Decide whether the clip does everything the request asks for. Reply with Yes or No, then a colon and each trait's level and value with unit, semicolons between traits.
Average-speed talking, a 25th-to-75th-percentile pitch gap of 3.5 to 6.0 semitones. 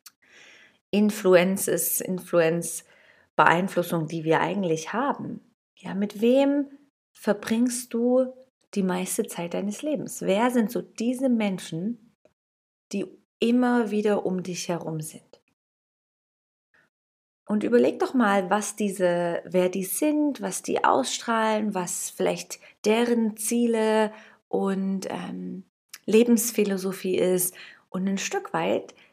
No: slow, 110 wpm; average, 4.5 semitones